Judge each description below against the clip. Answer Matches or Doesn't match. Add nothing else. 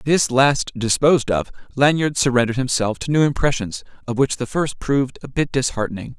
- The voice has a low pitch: Matches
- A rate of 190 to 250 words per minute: Doesn't match